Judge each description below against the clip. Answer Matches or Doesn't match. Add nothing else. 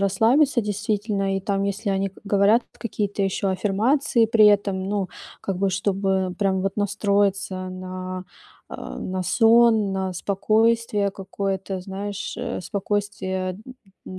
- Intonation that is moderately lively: Doesn't match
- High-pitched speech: Matches